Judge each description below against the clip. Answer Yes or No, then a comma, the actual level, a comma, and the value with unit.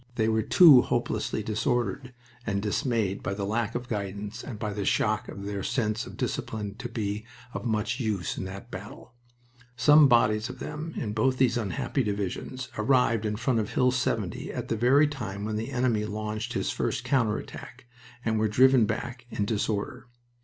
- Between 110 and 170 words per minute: No, average, 180 wpm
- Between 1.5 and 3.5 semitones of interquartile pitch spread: Yes, average, 3.1 semitones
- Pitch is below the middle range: Yes, low, 110 Hz